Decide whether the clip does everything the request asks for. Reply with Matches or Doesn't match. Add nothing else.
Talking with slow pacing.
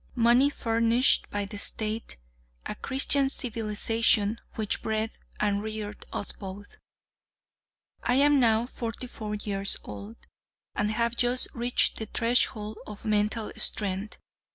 Matches